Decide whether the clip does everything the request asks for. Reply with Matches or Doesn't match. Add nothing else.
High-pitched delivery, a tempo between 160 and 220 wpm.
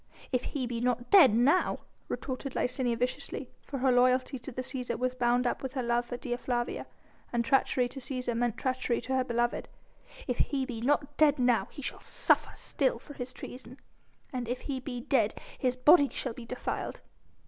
Matches